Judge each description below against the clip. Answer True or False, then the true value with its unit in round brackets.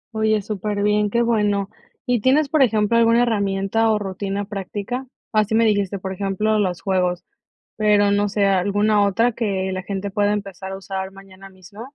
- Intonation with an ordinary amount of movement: False (2.0 semitones)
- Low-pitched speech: False (205 Hz)